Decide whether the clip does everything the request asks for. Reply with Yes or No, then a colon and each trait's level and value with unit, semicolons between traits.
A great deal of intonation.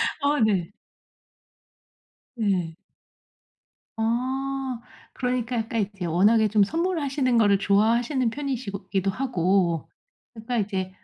No: average, 4.7 semitones